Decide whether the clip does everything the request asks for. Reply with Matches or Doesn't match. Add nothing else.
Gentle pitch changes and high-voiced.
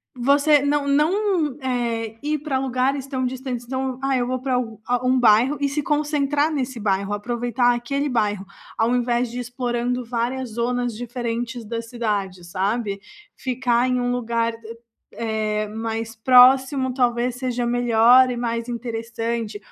Matches